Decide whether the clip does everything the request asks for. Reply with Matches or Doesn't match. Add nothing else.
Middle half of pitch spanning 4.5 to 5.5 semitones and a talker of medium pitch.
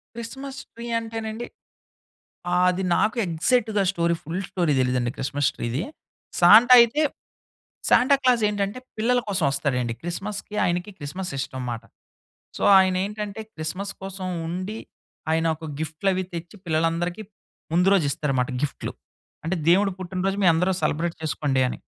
Matches